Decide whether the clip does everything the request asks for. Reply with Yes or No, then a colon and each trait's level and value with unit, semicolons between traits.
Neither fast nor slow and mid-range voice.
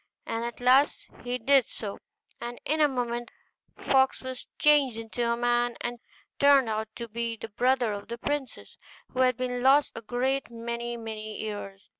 No: average, 180 wpm; high, 240 Hz